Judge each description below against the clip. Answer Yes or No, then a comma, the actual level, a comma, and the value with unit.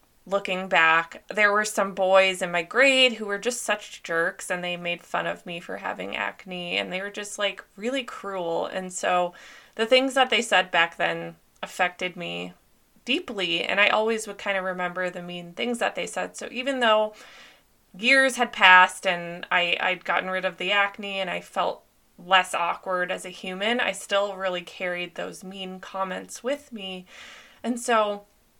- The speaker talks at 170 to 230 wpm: Yes, average, 185 wpm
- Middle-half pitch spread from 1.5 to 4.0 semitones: Yes, average, 2.9 semitones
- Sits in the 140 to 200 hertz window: Yes, high, 190 Hz